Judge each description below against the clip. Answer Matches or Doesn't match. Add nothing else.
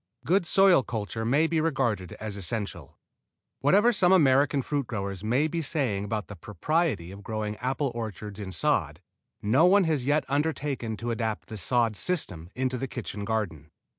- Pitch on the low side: Matches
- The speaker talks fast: Doesn't match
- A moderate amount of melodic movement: Doesn't match